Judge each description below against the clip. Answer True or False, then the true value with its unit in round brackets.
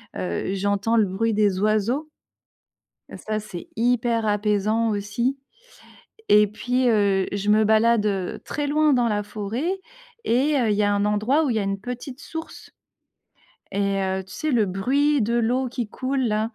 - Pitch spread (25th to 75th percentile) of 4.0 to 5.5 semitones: False (3.5 semitones)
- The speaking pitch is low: False (215 Hz)